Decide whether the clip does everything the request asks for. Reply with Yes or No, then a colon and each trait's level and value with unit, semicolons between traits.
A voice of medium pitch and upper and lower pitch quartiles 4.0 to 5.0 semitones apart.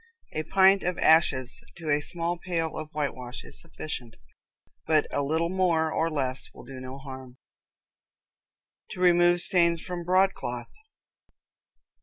Yes: medium, 160 Hz; average, 4.4 semitones